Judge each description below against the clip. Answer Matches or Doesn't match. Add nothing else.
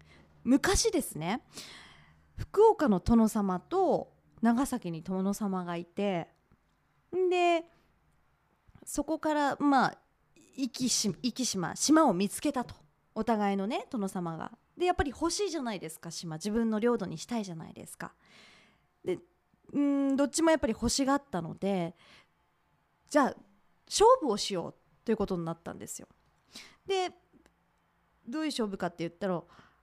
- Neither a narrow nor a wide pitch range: Doesn't match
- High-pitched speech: Matches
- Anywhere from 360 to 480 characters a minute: Doesn't match